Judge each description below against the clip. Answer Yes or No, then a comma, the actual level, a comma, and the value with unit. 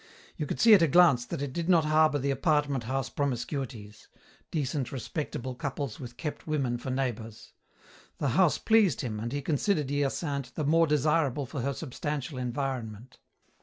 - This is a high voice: No, medium, 140 Hz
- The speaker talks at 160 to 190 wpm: Yes, average, 165 wpm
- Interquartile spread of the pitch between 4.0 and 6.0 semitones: No, average, 3.4 semitones